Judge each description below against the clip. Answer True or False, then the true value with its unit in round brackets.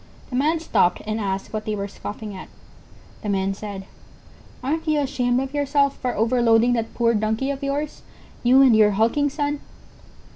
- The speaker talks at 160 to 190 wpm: True (170 wpm)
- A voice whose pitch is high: True (245 Hz)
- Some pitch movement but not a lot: True (4.7 semitones)